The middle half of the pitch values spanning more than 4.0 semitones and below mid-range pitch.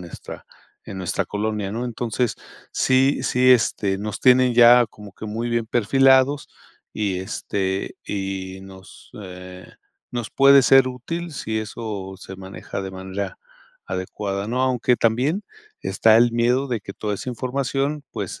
Yes: average, 4.6 semitones; low, 110 Hz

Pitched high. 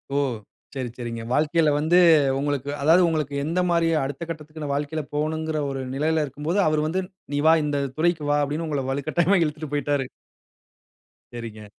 No: medium, 150 Hz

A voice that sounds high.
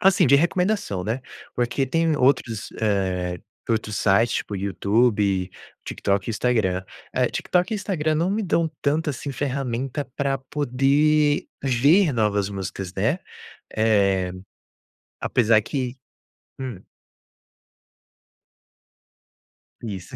No: low, 125 Hz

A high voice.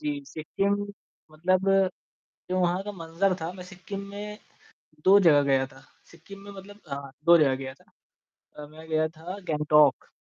No: medium, 170 Hz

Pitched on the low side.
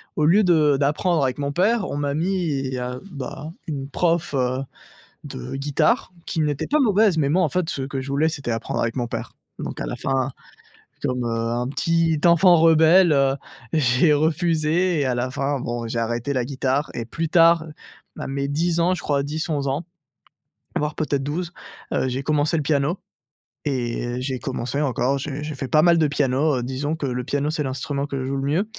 No: medium, 145 Hz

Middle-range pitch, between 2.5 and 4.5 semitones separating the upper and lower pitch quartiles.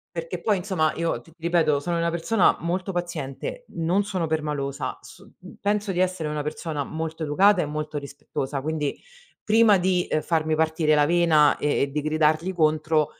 Yes: medium, 160 Hz; average, 2.8 semitones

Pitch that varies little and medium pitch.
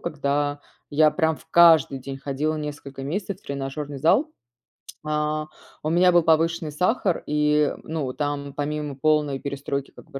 Yes: narrow, 2.2 semitones; medium, 150 Hz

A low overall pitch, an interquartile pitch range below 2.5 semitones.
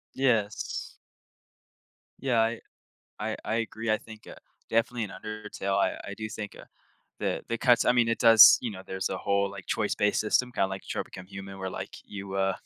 No: low, 110 Hz; average, 2.8 semitones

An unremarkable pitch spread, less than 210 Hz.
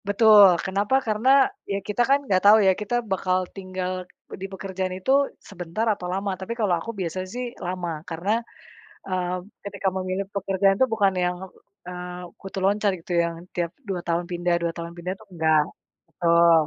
No: narrow, 2.2 semitones; medium, 185 Hz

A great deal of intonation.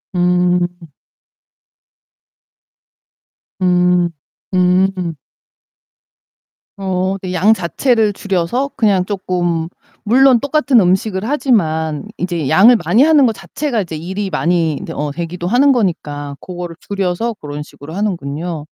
No: average, 4.1 semitones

